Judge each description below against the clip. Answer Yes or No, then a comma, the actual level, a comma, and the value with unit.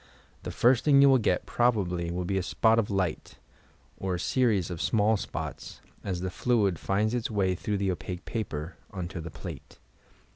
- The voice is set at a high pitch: No, very low, 95 Hz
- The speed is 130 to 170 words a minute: No, average, 185 wpm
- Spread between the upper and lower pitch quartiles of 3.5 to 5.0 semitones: Yes, average, 3.9 semitones